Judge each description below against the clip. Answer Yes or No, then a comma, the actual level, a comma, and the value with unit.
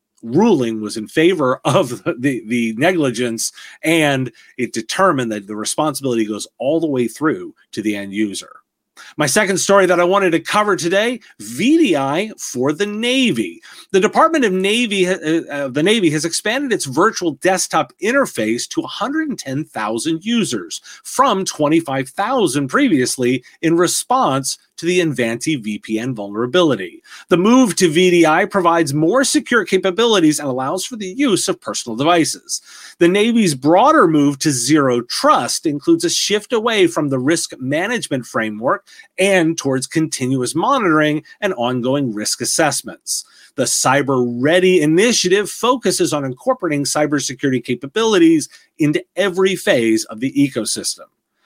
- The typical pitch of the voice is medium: Yes, medium, 165 Hz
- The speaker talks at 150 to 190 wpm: No, average, 140 wpm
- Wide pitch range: Yes, wide, 7.7 semitones